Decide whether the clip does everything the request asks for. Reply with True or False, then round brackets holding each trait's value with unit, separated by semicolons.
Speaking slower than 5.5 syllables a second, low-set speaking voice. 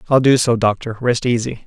False (5.6 syllables/s; 120 Hz)